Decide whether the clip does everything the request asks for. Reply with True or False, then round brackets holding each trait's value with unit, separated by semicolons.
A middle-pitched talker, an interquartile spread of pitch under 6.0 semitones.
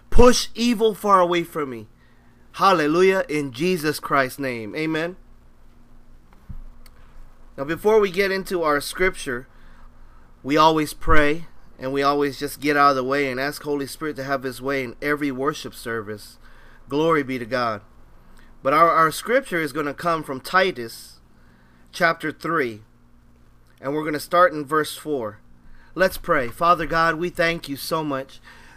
True (145 Hz; 5.5 semitones)